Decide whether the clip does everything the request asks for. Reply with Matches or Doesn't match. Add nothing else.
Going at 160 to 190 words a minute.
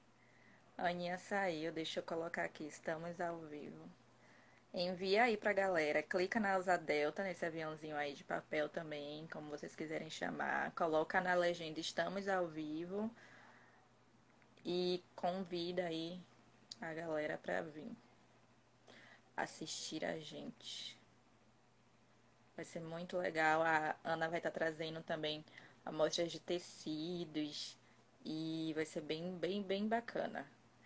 Doesn't match